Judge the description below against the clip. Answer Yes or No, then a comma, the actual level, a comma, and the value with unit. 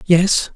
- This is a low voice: No, medium, 180 Hz